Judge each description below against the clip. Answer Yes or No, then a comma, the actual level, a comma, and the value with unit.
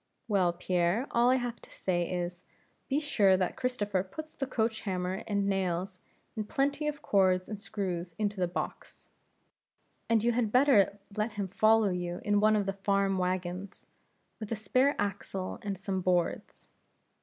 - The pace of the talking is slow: No, average, 165 wpm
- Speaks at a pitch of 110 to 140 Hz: No, high, 200 Hz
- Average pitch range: Yes, average, 3.3 semitones